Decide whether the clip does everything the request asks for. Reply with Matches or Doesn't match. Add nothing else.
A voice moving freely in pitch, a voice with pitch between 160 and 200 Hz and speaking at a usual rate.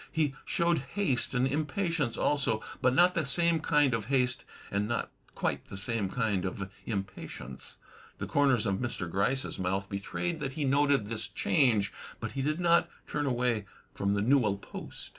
Doesn't match